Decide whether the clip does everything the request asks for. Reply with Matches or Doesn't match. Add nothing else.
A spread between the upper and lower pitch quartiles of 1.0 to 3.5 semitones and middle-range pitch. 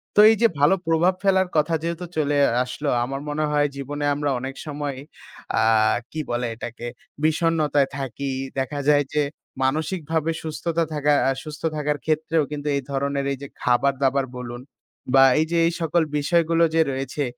Matches